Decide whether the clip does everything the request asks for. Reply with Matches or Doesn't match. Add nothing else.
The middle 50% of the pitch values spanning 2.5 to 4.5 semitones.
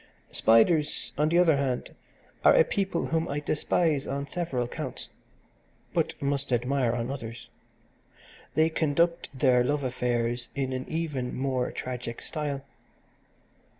Matches